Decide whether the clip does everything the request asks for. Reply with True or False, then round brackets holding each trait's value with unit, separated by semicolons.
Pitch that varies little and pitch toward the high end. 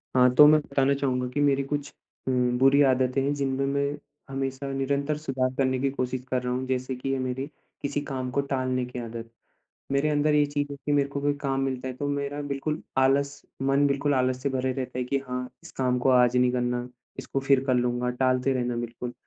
False (1.8 semitones; 135 Hz)